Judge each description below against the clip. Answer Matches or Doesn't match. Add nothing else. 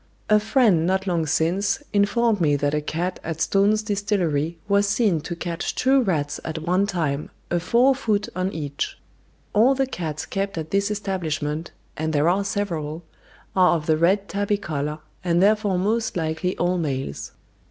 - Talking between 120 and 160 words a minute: Doesn't match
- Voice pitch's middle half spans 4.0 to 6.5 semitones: Matches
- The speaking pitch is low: Doesn't match